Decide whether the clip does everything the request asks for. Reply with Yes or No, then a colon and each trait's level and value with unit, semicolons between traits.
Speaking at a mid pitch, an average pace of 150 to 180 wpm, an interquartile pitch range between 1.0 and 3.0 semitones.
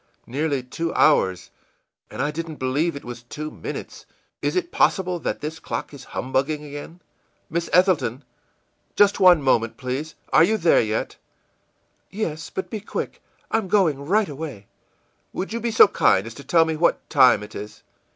No: medium, 155 Hz; average, 170 wpm; wide, 5.5 semitones